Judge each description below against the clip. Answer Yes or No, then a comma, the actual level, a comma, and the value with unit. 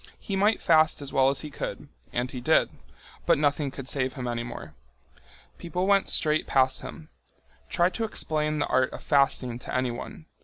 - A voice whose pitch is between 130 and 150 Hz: Yes, medium, 140 Hz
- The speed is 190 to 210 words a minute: No, average, 170 wpm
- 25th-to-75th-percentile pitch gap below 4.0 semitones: Yes, average, 3.6 semitones